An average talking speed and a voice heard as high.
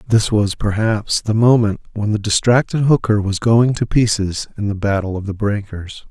No: average, 185 wpm; low, 110 Hz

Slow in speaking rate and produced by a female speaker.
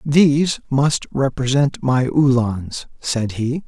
No: slow, 115 wpm; male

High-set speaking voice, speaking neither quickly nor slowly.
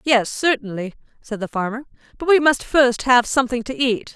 Yes: high, 245 Hz; average, 190 wpm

